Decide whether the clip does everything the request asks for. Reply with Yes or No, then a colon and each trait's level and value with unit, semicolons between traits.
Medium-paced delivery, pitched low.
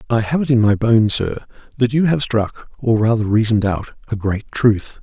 Yes: average, 190 wpm; low, 115 Hz